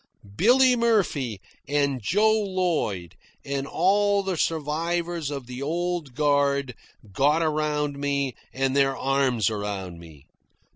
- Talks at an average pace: No, slow, 115 wpm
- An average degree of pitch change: Yes, average, 4.6 semitones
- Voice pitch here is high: No, medium, 145 Hz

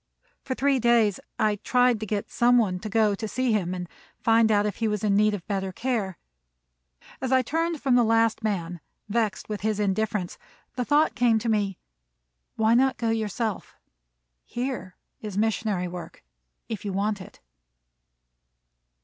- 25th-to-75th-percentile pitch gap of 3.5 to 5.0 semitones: No, average, 2.9 semitones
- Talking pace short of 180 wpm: Yes, average, 165 wpm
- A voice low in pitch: No, high, 220 Hz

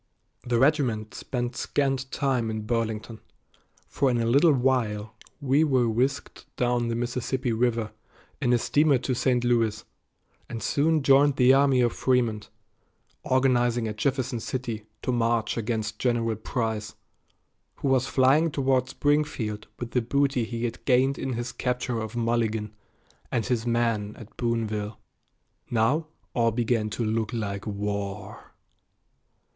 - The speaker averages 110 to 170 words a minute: Yes, average, 140 wpm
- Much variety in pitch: No, average, 2.8 semitones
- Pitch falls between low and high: No, low, 120 Hz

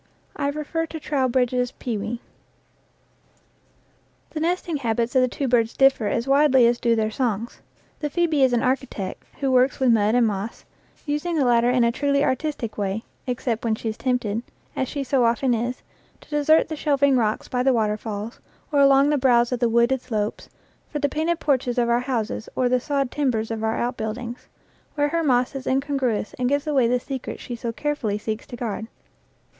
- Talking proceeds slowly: No, average, 195 wpm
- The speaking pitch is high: Yes, very high, 250 Hz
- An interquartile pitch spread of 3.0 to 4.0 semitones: Yes, average, 3.3 semitones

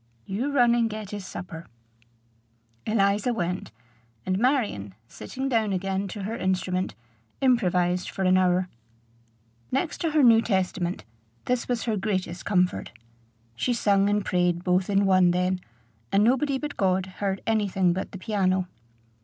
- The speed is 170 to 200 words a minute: No, average, 150 wpm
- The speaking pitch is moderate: No, high, 195 Hz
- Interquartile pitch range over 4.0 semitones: No, average, 3.7 semitones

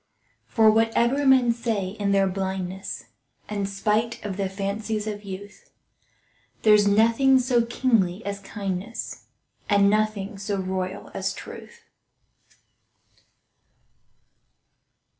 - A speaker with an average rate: No, slow, 105 wpm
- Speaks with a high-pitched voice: Yes, high, 205 Hz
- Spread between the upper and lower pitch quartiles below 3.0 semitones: Yes, narrow, 2.6 semitones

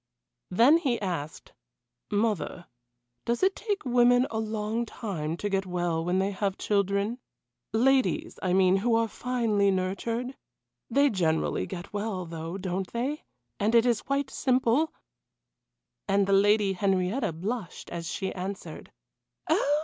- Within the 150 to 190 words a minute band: No, average, 140 wpm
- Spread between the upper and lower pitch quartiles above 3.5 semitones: Yes, average, 4.4 semitones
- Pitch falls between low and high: No, high, 205 Hz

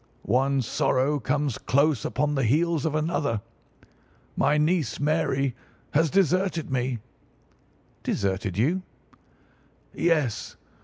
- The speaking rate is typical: No, slow, 100 wpm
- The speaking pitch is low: No, medium, 145 Hz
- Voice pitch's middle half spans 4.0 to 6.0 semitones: No, average, 3.6 semitones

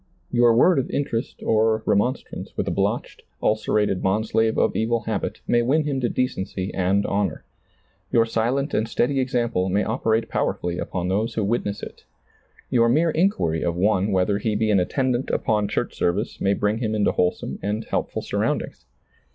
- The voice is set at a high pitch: No, low, 110 Hz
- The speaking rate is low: No, average, 170 wpm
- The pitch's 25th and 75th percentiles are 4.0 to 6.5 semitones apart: No, average, 3.2 semitones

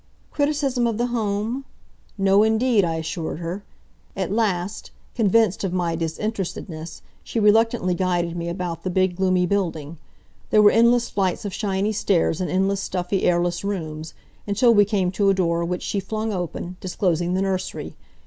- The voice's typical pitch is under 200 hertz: Yes, high, 190 Hz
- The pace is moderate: Yes, average, 160 wpm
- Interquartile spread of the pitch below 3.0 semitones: No, average, 3.3 semitones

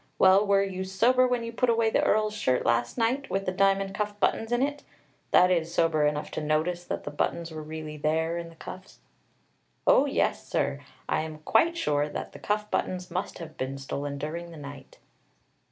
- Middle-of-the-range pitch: Yes, medium, 180 Hz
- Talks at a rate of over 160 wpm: Yes, average, 200 wpm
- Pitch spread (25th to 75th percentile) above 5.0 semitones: Yes, wide, 5.4 semitones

